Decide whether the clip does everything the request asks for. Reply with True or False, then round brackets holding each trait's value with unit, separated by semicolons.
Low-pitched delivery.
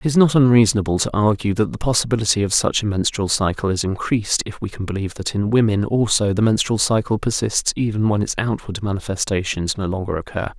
True (105 Hz)